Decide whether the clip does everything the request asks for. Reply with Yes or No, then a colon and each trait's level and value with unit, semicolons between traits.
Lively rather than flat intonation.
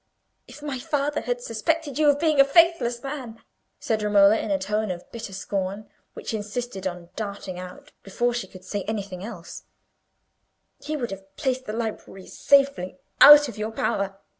Yes: wide, 6.0 semitones